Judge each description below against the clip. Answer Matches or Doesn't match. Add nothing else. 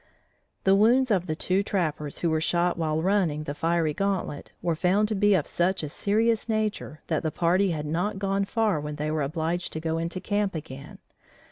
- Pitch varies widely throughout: Doesn't match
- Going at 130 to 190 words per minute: Doesn't match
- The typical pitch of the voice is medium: Matches